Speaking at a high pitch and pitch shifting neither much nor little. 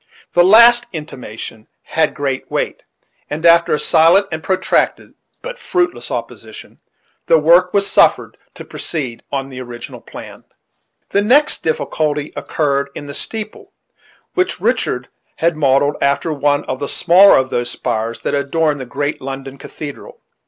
No: medium, 150 Hz; average, 4.3 semitones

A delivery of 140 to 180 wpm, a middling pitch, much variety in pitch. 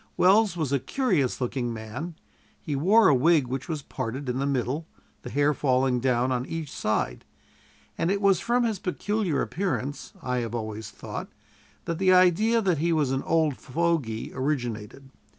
Yes: average, 170 wpm; medium, 145 Hz; wide, 5.7 semitones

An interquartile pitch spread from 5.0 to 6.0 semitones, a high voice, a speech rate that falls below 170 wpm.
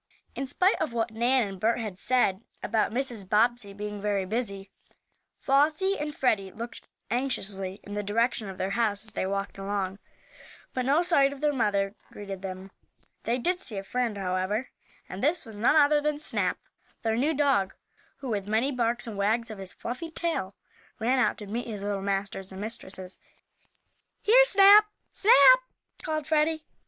No: wide, 5.6 semitones; high, 225 Hz; average, 175 wpm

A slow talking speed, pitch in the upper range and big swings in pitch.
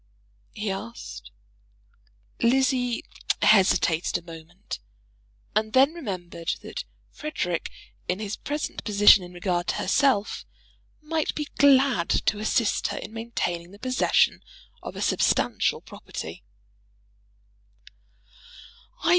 Yes: slow, 105 wpm; high, 210 Hz; wide, 6.5 semitones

